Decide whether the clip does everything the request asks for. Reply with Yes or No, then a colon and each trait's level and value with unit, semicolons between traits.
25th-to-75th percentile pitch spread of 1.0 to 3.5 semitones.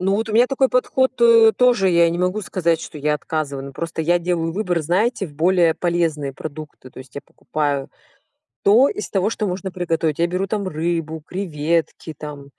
No: average, 3.9 semitones